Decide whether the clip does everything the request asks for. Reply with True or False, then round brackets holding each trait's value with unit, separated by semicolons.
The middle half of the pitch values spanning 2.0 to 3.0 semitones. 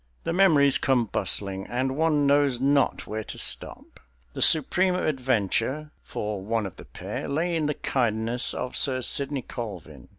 False (4.8 semitones)